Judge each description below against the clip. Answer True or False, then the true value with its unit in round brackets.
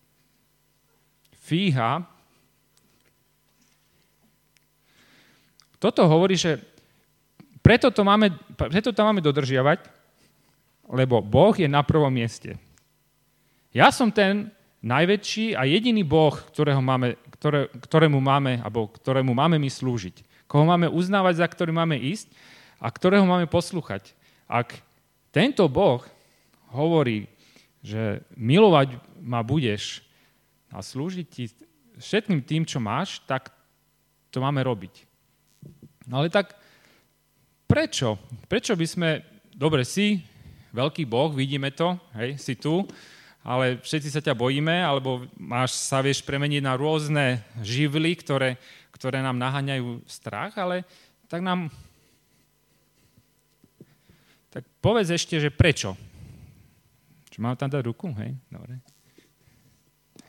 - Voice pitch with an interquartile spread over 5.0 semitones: True (5.5 semitones)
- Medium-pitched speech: True (145 Hz)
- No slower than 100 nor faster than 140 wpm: True (110 wpm)